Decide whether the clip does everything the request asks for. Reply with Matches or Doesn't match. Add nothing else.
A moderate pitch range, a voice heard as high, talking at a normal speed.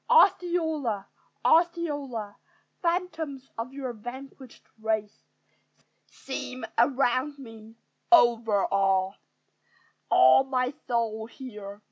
Doesn't match